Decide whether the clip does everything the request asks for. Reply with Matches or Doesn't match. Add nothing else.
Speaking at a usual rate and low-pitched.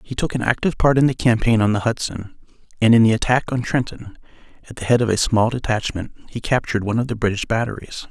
Doesn't match